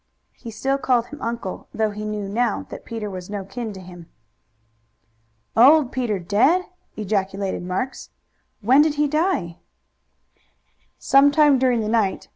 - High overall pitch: Yes, high, 225 Hz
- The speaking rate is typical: Yes, average, 145 wpm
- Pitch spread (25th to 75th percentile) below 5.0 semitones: No, average, 5.3 semitones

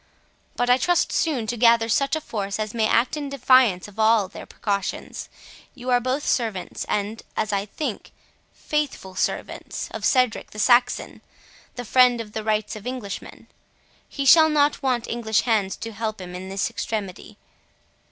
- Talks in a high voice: Yes, high, 230 Hz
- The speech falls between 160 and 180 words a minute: Yes, average, 170 wpm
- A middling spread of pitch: Yes, average, 3.4 semitones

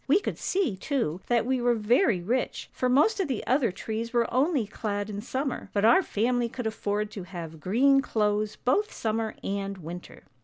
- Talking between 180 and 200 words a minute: Yes, average, 190 wpm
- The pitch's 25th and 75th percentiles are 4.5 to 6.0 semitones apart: No, average, 4.1 semitones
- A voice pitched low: No, high, 225 Hz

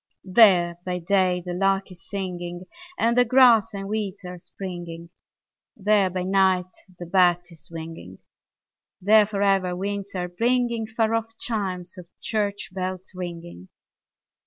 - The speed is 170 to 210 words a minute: No, average, 140 wpm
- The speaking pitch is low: No, high, 190 Hz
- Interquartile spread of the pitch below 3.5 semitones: Yes, average, 2.8 semitones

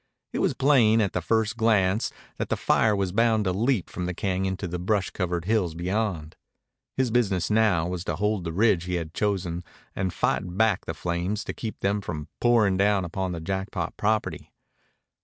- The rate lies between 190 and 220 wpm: Yes, average, 195 wpm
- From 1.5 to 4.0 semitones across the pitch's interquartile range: Yes, average, 3.5 semitones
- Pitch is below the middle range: Yes, very low, 95 Hz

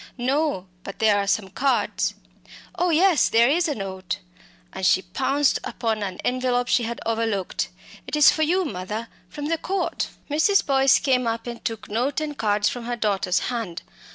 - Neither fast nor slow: Yes, average, 180 wpm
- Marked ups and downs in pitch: Yes, wide, 5.8 semitones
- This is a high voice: Yes, high, 240 Hz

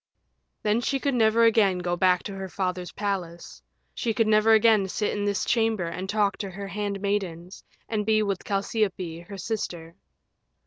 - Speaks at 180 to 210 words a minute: No, average, 170 wpm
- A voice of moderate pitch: No, high, 200 Hz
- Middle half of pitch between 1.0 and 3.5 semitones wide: Yes, average, 2.8 semitones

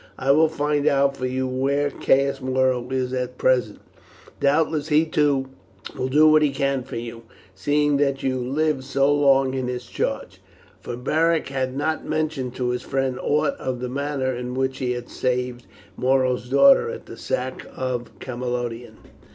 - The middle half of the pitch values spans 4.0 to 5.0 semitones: No, narrow, 2.4 semitones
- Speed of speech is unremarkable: Yes, average, 170 wpm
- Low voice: Yes, low, 130 Hz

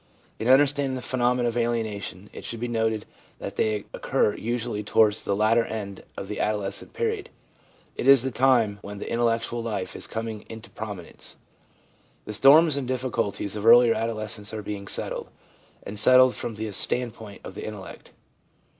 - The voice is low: Yes, low, 115 Hz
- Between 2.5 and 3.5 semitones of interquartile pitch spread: Yes, average, 2.8 semitones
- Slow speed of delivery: No, average, 165 wpm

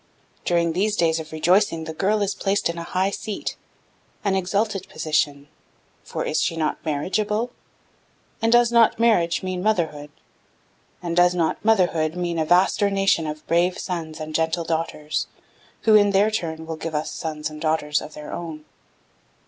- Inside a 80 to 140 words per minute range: No, average, 170 wpm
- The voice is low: No, medium, 170 Hz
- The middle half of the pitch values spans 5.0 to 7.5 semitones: No, average, 4.0 semitones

